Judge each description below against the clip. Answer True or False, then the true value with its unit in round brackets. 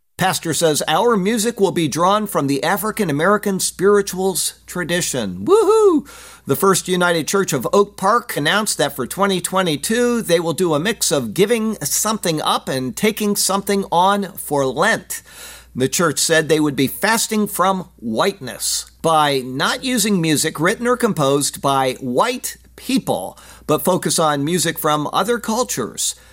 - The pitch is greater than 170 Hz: True (185 Hz)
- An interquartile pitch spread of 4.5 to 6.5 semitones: True (5.3 semitones)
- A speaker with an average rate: True (150 wpm)